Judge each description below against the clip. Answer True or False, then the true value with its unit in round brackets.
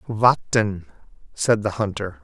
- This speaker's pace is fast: False (105 wpm)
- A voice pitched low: True (105 Hz)